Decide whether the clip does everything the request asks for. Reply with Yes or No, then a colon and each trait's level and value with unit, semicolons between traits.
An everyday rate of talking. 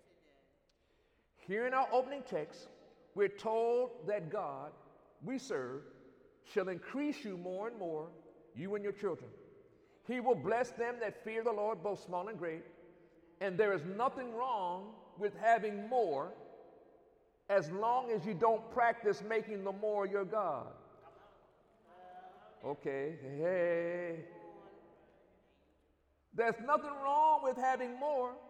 No: slow, 125 wpm